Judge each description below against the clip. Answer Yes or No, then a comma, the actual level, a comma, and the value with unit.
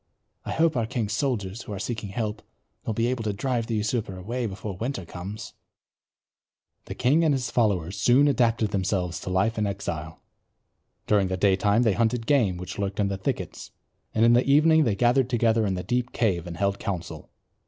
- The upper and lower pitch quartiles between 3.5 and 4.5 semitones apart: Yes, average, 3.9 semitones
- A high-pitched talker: No, low, 110 Hz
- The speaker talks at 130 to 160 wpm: No, average, 190 wpm